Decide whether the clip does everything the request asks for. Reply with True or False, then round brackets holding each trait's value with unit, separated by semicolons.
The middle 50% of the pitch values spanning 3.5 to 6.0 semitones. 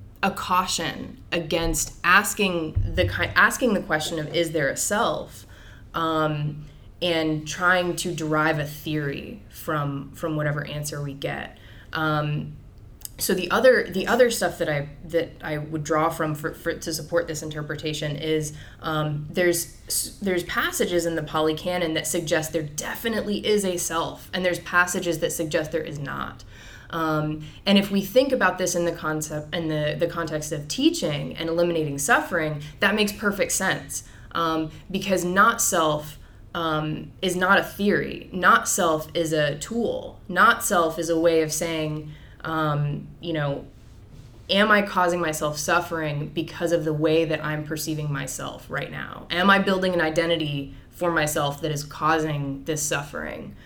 False (2.5 semitones)